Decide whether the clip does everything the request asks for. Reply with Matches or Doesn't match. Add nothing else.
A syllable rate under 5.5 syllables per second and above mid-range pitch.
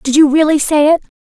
Doesn't match